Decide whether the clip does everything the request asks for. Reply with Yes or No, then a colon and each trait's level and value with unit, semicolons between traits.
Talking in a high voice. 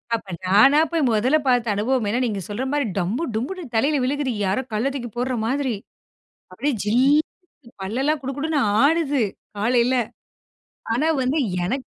Yes: very high, 255 Hz